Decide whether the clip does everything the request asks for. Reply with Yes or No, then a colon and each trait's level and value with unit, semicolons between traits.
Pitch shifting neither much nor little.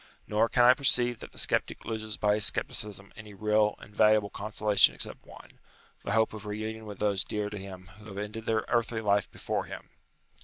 No: narrow, 1.3 semitones